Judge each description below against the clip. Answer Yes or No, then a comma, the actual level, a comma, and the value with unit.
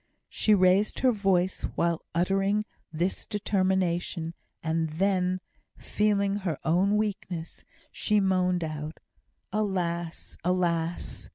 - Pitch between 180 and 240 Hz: Yes, medium, 185 Hz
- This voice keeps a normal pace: No, slow, 100 wpm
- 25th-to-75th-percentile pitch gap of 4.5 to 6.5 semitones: No, average, 2.8 semitones